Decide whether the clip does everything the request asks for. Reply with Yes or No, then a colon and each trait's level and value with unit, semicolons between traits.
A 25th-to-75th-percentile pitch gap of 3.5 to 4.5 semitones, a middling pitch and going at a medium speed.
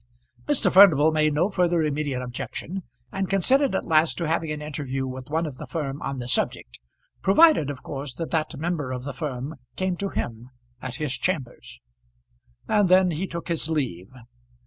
No: average, 4.9 semitones; medium, 155 Hz; average, 180 wpm